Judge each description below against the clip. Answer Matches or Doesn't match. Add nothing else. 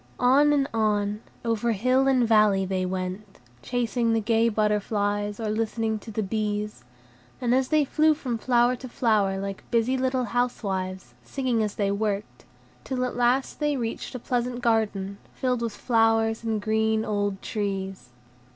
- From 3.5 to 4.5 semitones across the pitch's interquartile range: Doesn't match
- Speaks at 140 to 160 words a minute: Matches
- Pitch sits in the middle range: Doesn't match